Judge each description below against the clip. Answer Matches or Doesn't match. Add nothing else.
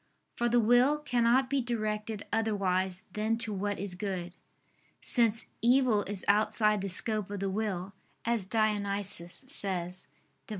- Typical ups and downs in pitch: Matches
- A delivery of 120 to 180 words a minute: Matches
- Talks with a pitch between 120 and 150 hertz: Doesn't match